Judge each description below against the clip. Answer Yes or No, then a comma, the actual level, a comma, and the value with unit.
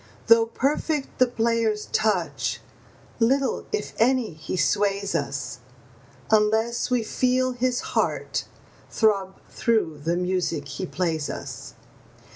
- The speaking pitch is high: Yes, high, 215 Hz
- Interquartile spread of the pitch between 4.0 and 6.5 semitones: Yes, average, 5.2 semitones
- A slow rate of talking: Yes, slow, 110 wpm